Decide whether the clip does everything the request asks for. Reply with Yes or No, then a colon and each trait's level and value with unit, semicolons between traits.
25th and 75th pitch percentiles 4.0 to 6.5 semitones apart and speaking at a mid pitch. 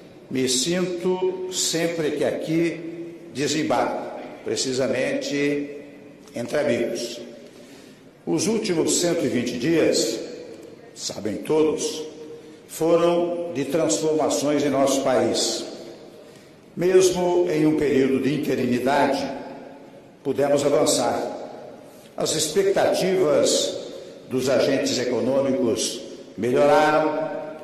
No: average, 3.2 semitones; medium, 155 Hz